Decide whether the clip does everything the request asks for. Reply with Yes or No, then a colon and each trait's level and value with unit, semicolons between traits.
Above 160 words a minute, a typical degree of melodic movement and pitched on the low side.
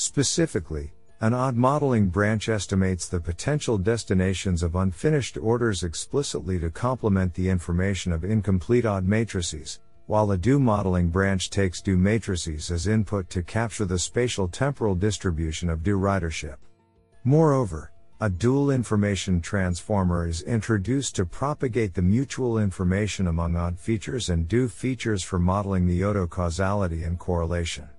No: average, 140 wpm; average, 4.1 semitones; low, 100 Hz